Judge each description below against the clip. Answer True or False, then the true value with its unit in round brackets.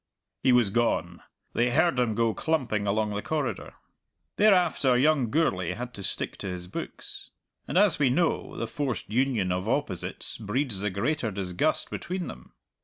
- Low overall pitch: True (120 Hz)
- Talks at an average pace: True (165 wpm)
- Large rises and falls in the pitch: True (6.4 semitones)